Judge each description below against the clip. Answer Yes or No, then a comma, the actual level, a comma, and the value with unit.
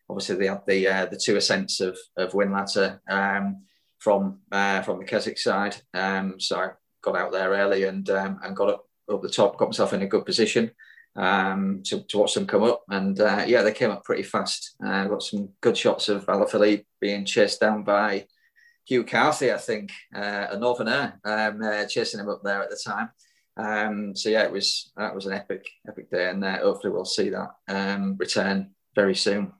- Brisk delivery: Yes, fast, 210 wpm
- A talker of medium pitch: No, low, 100 Hz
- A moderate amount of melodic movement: No, narrow, 1.3 semitones